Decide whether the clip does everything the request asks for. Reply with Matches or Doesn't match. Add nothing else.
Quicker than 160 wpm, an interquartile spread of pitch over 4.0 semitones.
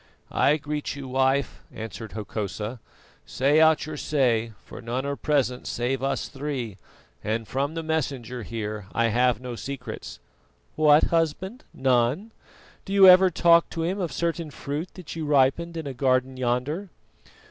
Doesn't match